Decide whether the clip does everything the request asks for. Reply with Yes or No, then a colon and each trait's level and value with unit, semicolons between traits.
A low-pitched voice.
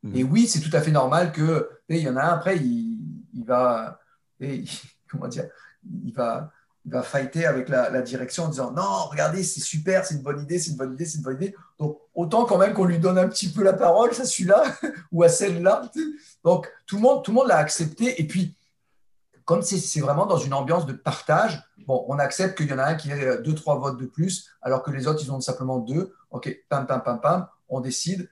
No: medium, 165 Hz